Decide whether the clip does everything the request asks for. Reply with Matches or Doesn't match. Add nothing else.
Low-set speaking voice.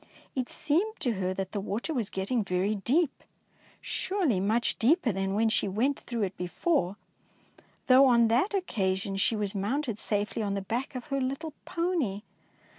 Doesn't match